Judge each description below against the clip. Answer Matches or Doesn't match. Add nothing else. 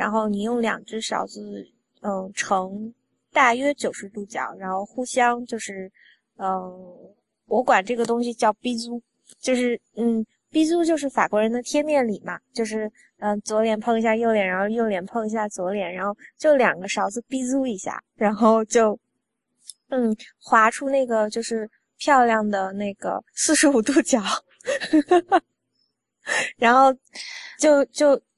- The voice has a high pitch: Matches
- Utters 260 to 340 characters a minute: Doesn't match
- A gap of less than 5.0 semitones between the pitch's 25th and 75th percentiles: Matches